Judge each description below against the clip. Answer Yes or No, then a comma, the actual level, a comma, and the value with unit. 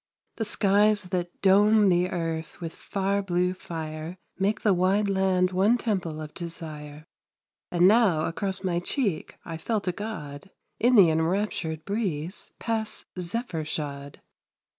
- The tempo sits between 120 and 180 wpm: Yes, average, 140 wpm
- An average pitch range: Yes, average, 4.0 semitones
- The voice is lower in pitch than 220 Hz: Yes, medium, 185 Hz